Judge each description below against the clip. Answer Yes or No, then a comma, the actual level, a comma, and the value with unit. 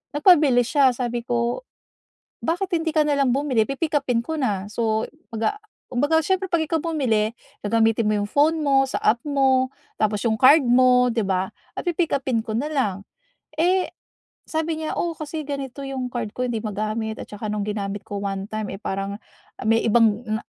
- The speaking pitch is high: Yes, high, 245 Hz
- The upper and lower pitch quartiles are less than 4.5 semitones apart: No, average, 5.3 semitones